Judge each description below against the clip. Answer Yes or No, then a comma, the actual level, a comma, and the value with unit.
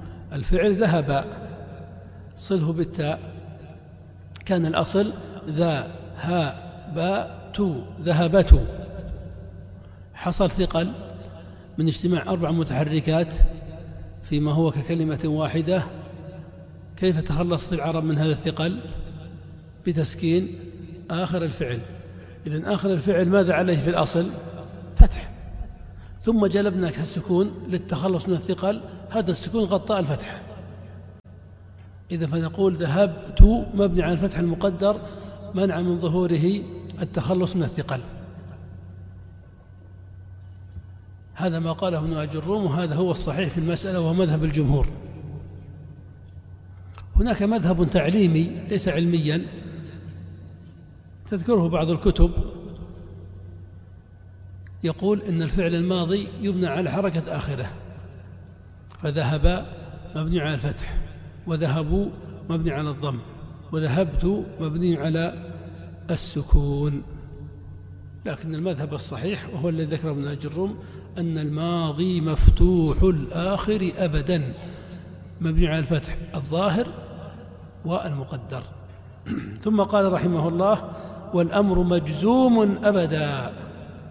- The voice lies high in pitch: No, medium, 160 Hz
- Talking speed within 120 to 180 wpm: No, average, 90 wpm